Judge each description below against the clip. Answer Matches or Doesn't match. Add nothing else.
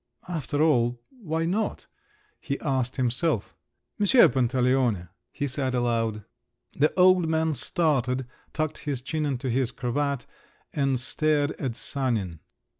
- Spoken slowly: Matches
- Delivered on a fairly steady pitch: Doesn't match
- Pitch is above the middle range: Doesn't match